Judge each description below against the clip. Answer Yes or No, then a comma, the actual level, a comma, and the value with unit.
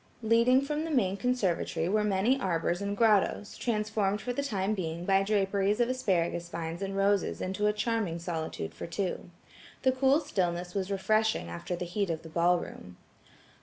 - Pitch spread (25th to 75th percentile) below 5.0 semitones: Yes, average, 3.9 semitones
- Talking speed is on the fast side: No, average, 175 wpm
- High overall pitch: Yes, high, 195 Hz